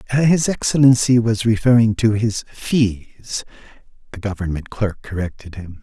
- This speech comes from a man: Yes, male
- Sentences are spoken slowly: Yes, slow, 125 wpm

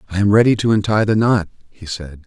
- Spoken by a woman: No, male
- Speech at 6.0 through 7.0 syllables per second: Yes, 6.2 syllables/s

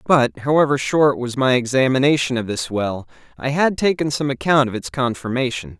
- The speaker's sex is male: Yes, male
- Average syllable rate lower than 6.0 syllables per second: Yes, 5.2 syllables/s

